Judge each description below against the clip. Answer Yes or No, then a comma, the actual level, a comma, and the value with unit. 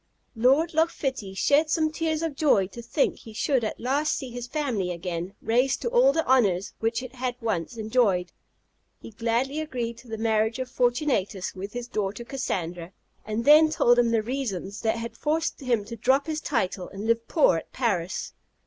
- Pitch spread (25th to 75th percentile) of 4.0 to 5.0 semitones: Yes, average, 4.6 semitones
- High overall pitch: Yes, high, 235 Hz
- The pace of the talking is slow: No, average, 190 wpm